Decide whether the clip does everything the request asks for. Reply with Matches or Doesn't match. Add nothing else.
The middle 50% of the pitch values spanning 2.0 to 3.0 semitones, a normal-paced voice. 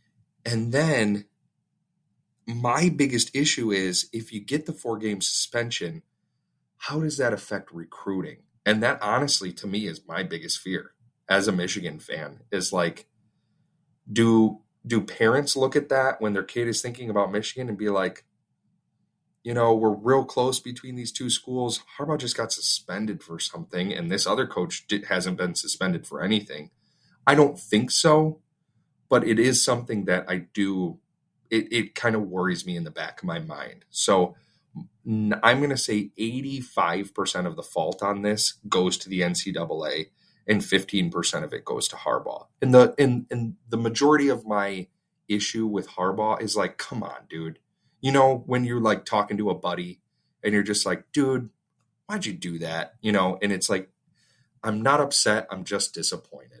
Doesn't match